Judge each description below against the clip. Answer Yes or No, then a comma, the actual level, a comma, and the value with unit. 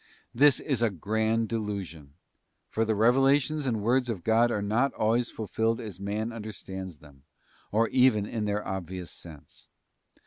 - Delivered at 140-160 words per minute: Yes, average, 150 wpm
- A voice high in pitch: No, low, 110 Hz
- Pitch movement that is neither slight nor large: Yes, average, 3.1 semitones